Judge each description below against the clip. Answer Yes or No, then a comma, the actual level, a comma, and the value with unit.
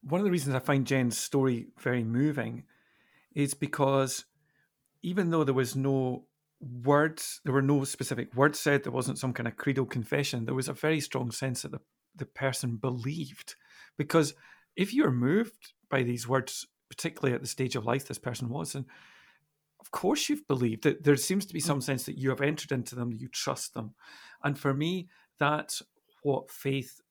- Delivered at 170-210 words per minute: Yes, average, 190 wpm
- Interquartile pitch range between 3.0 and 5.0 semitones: No, narrow, 2.5 semitones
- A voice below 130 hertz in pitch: No, low, 135 Hz